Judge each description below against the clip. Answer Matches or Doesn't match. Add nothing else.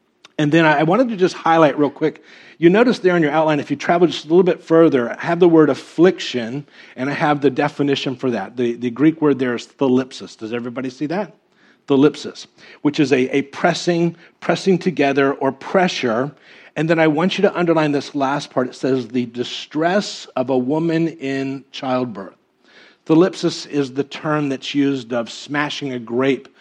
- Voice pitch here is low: Doesn't match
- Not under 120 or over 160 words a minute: Doesn't match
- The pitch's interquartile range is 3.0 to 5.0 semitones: Matches